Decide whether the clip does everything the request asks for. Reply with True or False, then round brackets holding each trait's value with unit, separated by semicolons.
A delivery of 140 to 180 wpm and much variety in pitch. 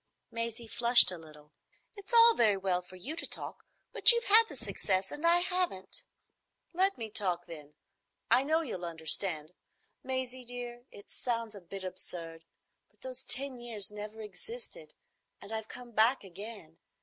True (160 wpm; 5.8 semitones)